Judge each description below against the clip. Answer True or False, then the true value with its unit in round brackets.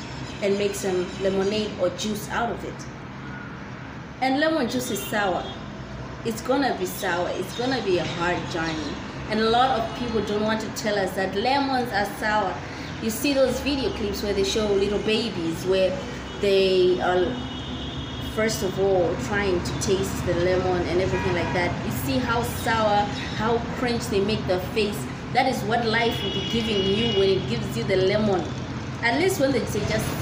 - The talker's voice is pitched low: False (200 Hz)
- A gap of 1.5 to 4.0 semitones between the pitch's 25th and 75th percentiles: True (3.6 semitones)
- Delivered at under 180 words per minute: False (185 wpm)